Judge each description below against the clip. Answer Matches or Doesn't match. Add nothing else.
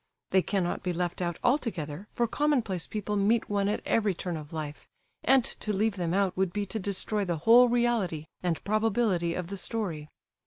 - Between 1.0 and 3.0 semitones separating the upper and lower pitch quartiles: Doesn't match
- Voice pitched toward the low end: Doesn't match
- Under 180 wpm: Doesn't match